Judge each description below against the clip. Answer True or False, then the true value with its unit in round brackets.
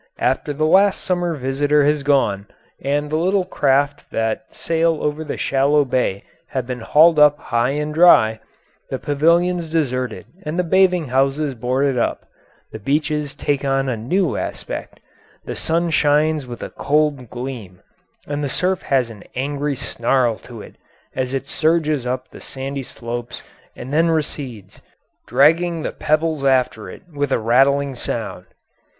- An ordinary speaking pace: True (155 wpm)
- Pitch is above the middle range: False (140 Hz)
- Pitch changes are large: False (3.5 semitones)